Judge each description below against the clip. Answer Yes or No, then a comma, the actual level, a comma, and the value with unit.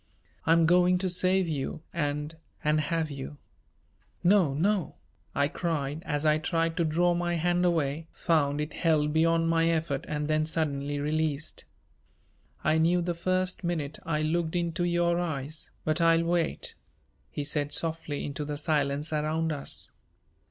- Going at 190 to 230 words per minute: No, average, 150 wpm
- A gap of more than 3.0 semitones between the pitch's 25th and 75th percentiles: No, narrow, 2.5 semitones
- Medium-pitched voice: Yes, medium, 160 Hz